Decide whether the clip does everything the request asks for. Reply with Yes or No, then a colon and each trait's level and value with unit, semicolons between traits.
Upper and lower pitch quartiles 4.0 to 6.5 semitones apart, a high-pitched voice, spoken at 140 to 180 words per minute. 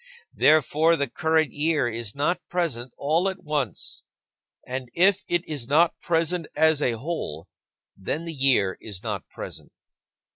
No: wide, 5.4 semitones; medium, 150 Hz; average, 145 wpm